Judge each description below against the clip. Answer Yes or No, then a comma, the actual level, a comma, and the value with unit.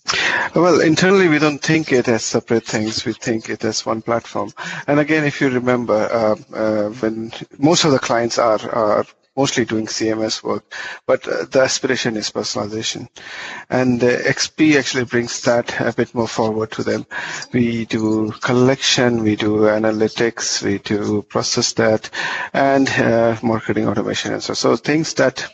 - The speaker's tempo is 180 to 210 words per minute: No, average, 165 wpm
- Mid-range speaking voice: No, low, 120 Hz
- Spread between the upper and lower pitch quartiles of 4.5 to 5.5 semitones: No, average, 3.4 semitones